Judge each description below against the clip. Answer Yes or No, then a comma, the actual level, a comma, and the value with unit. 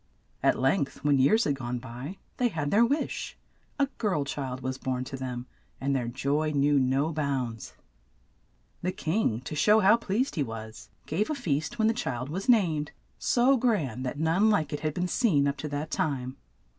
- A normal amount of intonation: No, wide, 7.1 semitones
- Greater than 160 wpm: Yes, average, 195 wpm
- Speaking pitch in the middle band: Yes, medium, 145 Hz